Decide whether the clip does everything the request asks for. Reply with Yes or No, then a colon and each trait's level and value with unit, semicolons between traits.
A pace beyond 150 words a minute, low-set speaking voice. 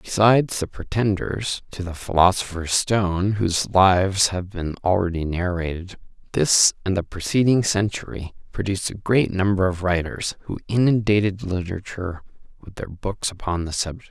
No: average, 140 wpm; very low, 95 Hz